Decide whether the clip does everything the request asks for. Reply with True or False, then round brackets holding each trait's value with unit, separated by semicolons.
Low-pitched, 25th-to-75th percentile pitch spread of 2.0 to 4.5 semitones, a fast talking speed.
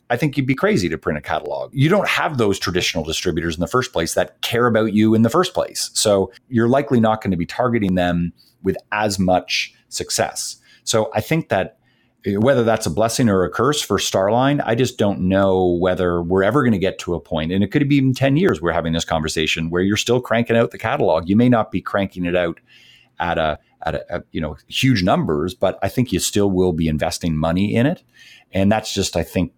False (100 Hz; 4.9 semitones; 235 wpm)